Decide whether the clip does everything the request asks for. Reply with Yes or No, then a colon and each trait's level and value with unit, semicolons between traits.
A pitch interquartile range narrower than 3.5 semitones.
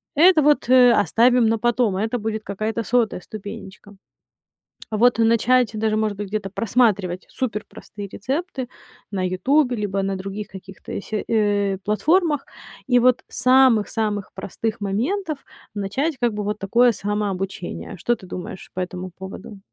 No: average, 3.8 semitones